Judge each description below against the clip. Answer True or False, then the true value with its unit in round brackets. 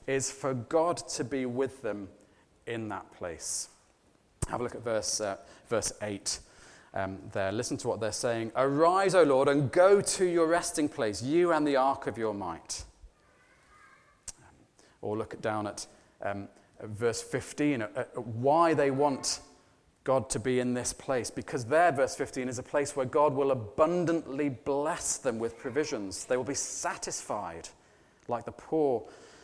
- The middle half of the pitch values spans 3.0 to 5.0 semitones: False (5.6 semitones)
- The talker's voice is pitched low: True (130 Hz)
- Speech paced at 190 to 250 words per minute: False (165 wpm)